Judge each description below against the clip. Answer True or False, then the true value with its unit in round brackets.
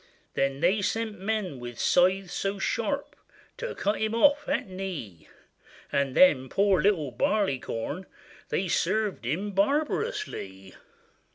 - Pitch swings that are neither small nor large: False (7.3 semitones)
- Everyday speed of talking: False (120 wpm)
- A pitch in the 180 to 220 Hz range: True (190 Hz)